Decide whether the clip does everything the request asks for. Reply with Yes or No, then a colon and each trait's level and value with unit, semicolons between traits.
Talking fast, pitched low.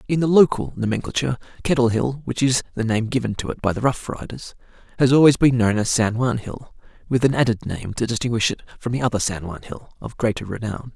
Yes: fast, 225 wpm; low, 120 Hz